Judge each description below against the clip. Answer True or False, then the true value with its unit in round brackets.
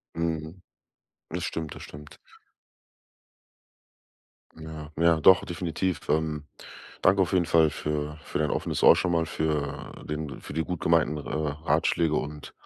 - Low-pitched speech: True (80 Hz)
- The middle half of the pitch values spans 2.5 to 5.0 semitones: False (1.8 semitones)